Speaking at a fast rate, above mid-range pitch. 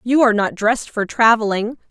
No: average, 190 wpm; high, 225 Hz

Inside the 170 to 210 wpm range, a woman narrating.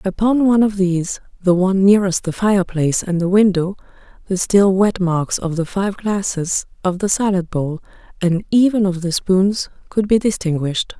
Yes: average, 175 wpm; female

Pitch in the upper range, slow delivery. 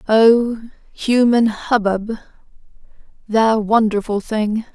Yes: high, 220 Hz; slow, 75 wpm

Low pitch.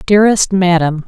No: medium, 185 Hz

